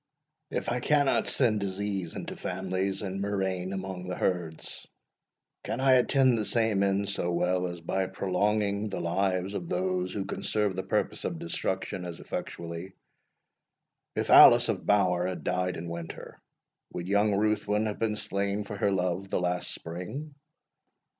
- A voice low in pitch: Yes, very low, 95 Hz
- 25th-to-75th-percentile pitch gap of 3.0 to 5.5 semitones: No, narrow, 2.5 semitones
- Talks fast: No, average, 160 wpm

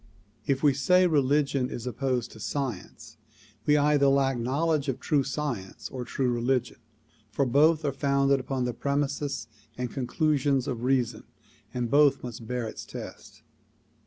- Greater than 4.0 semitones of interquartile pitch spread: No, narrow, 2.5 semitones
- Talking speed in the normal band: Yes, average, 150 wpm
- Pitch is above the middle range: No, low, 135 Hz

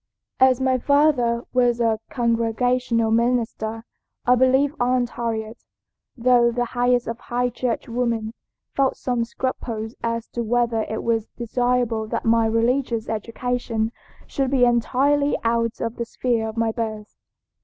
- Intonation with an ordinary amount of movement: No, narrow, 1.7 semitones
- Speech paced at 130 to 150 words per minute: Yes, average, 140 wpm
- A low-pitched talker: No, high, 235 Hz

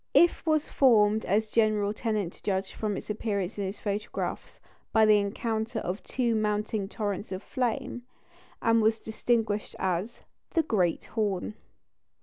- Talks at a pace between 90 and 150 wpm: Yes, average, 140 wpm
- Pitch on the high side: Yes, high, 215 Hz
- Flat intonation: Yes, narrow, 2.0 semitones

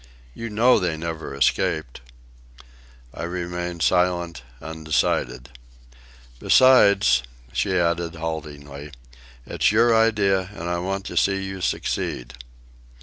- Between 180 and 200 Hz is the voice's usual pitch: No, very low, 85 Hz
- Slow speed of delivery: Yes, slow, 105 wpm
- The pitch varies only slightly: No, average, 3.6 semitones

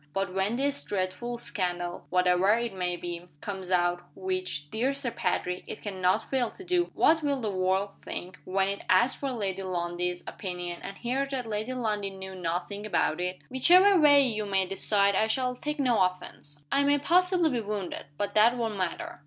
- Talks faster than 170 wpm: Yes, average, 190 wpm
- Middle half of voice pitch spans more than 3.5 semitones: Yes, wide, 5.4 semitones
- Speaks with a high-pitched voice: Yes, high, 200 Hz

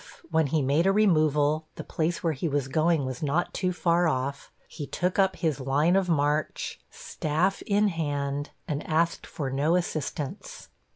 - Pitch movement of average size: Yes, average, 3.3 semitones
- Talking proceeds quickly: No, average, 175 wpm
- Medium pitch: Yes, medium, 155 Hz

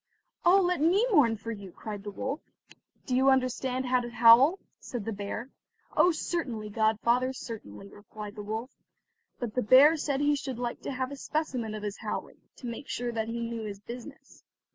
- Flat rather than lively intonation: No, average, 3.8 semitones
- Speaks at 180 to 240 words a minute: Yes, average, 190 wpm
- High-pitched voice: Yes, high, 245 Hz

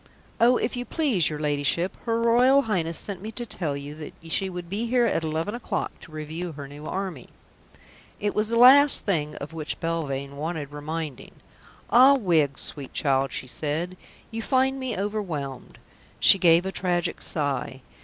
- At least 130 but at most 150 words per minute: No, average, 175 wpm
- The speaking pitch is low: No, medium, 170 Hz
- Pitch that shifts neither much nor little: No, wide, 7.1 semitones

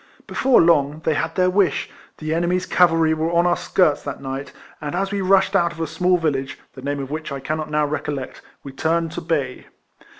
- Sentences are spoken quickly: Yes, fast, 210 wpm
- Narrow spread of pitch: No, average, 3.3 semitones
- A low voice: No, medium, 160 Hz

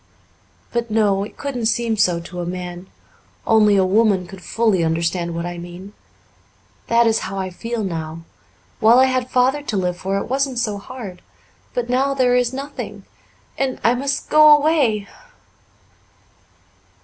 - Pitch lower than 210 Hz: No, high, 220 Hz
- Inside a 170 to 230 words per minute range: No, average, 160 wpm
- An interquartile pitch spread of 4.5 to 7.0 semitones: Yes, average, 5.3 semitones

